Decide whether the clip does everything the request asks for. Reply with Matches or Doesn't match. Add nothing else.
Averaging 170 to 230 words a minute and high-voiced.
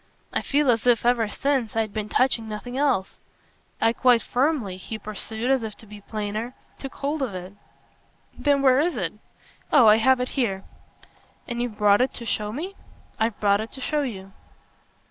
Matches